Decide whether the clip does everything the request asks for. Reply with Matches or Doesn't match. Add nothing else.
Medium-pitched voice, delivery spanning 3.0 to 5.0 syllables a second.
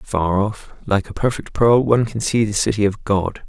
Doesn't match